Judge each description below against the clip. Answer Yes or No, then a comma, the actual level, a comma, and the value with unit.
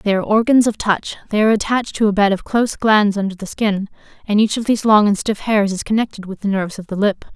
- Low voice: No, high, 205 Hz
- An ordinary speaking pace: No, fast, 270 wpm